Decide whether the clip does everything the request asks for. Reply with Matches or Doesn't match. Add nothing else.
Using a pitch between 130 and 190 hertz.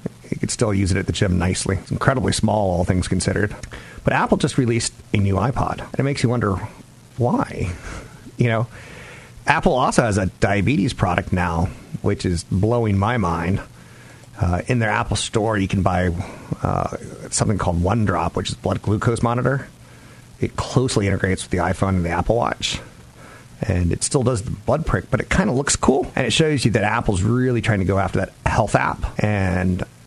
Doesn't match